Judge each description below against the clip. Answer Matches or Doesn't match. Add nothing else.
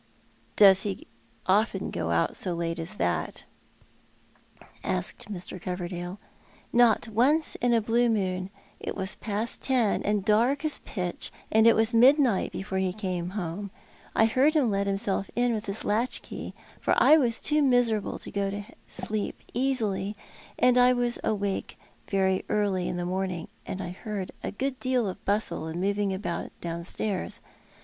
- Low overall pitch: Doesn't match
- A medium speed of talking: Matches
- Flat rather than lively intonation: Doesn't match